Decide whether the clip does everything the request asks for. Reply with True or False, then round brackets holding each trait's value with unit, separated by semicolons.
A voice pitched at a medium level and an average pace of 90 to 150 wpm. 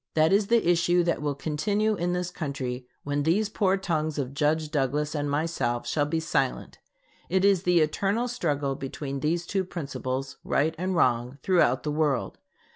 False (155 Hz; 175 wpm)